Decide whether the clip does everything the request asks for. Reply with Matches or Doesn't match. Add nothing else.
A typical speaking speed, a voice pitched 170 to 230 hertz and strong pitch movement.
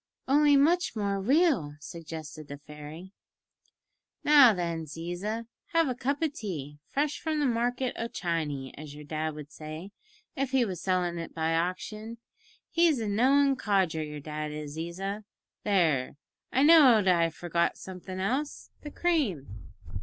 Matches